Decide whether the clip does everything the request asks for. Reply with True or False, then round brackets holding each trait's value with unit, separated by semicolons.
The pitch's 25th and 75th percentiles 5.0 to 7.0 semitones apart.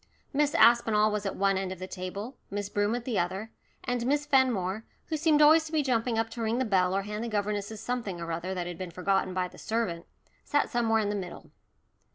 False (4.3 semitones)